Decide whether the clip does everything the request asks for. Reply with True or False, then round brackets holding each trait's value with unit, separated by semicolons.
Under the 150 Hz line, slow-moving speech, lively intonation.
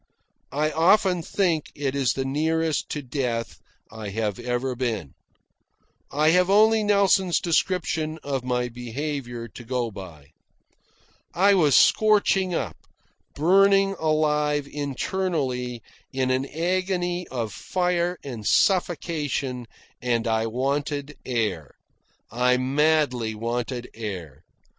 True (140 Hz; 110 wpm; 5.9 semitones)